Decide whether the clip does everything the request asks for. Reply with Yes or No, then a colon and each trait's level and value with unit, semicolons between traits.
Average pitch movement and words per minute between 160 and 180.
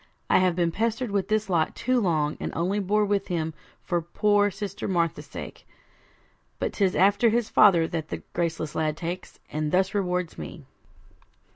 Yes: average, 3.6 semitones; average, 170 wpm